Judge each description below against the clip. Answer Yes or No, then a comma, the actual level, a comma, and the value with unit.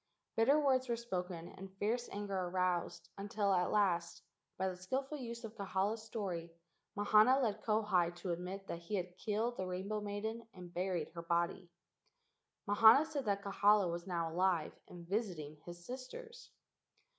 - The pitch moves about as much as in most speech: Yes, average, 4.0 semitones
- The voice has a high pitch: Yes, high, 195 Hz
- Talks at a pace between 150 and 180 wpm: Yes, average, 155 wpm